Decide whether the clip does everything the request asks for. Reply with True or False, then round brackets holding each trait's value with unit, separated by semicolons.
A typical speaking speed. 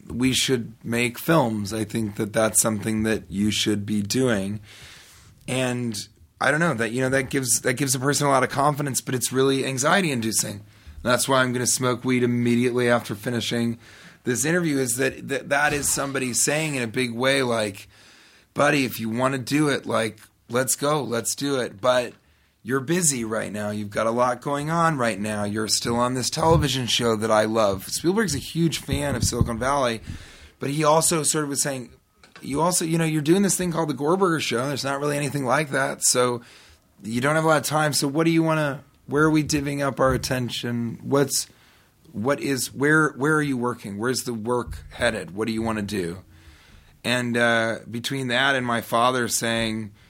False (210 wpm)